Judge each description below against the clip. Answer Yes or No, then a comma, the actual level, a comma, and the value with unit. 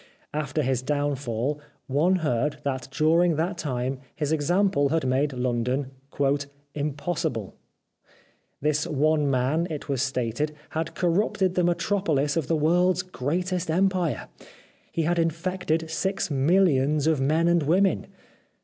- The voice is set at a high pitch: No, medium, 155 Hz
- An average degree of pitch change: Yes, average, 3.8 semitones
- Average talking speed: No, slow, 130 wpm